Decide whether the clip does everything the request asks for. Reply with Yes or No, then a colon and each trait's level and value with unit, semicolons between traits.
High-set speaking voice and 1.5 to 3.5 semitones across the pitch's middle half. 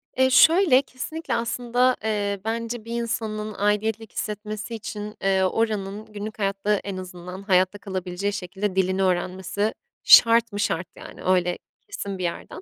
Yes: high, 210 Hz; average, 3.1 semitones